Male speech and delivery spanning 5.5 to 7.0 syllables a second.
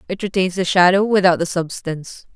No: female; 5.7 syllables/s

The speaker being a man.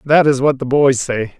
Yes: male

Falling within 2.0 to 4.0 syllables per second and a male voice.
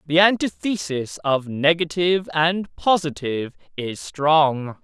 Yes: 3.9 syllables/s; male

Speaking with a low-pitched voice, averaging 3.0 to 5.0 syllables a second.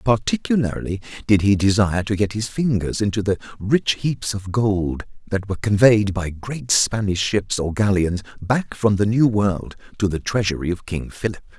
Yes: low, 105 Hz; 4.8 syllables/s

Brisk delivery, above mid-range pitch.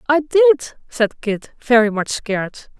No: average, 150 wpm; very high, 250 Hz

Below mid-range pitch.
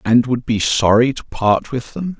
Yes: low, 125 Hz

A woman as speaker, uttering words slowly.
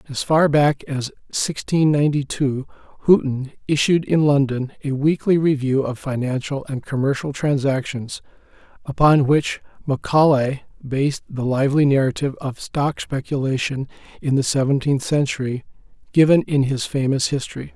No: male; slow, 130 wpm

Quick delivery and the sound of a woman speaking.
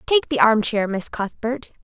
No: average, 165 wpm; female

